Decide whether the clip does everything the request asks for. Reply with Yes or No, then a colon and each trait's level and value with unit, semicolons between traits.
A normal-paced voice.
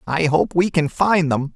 No: fast, 230 wpm